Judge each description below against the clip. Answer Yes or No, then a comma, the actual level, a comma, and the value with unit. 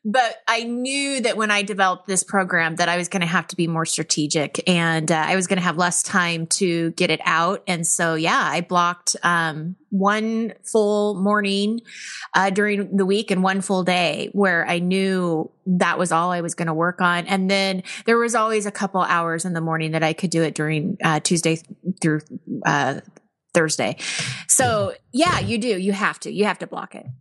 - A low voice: No, medium, 180 Hz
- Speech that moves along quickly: Yes, fast, 210 wpm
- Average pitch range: Yes, average, 3.4 semitones